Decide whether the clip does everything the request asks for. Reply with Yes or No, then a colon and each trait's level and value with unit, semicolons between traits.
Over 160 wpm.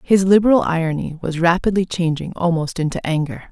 No: average, 155 wpm